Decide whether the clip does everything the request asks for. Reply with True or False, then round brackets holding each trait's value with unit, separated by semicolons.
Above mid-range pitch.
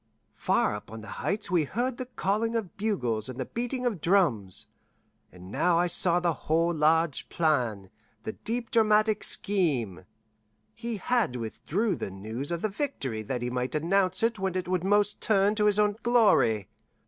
False (180 Hz)